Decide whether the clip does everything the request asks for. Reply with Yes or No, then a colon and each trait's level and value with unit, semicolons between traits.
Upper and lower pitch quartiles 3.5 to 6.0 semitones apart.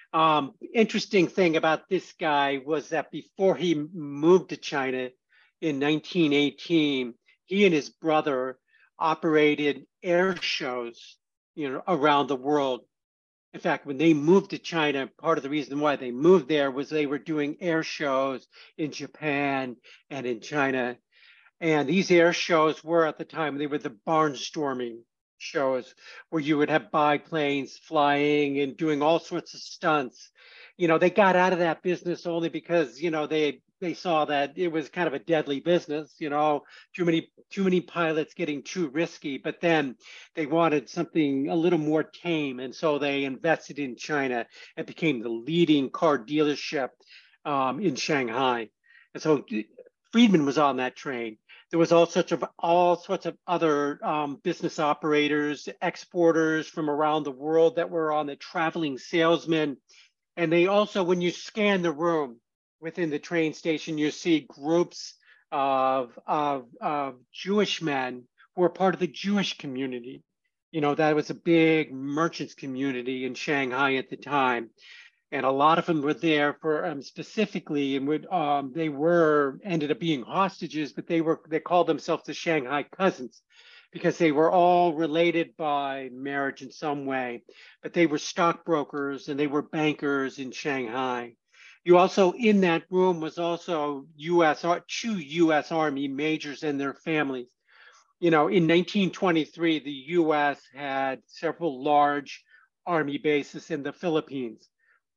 No: average, 3.1 semitones